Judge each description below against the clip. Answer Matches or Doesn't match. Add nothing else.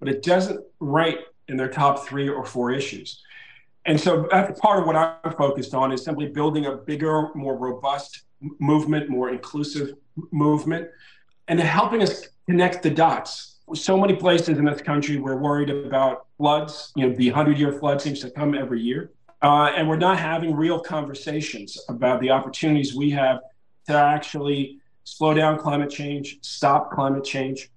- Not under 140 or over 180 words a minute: Matches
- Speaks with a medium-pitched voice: Matches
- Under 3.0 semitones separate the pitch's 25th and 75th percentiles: Matches